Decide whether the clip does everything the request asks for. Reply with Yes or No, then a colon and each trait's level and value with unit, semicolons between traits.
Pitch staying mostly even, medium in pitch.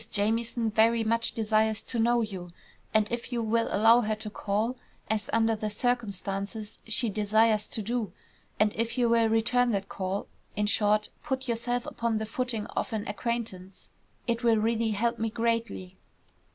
No: narrow, 1.8 semitones; high, 225 Hz